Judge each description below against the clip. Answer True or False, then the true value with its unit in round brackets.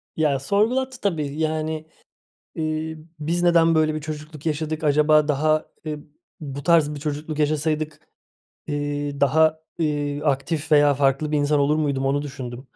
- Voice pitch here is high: False (150 Hz)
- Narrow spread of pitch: True (1.5 semitones)